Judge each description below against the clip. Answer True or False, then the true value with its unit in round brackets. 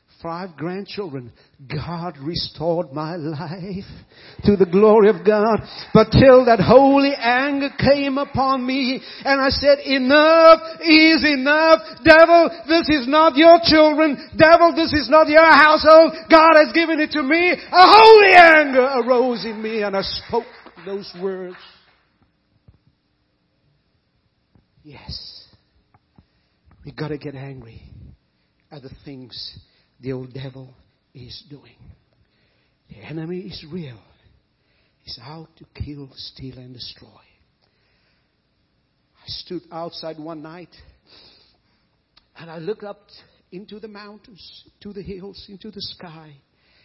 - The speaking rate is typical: False (125 wpm)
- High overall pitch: True (205 Hz)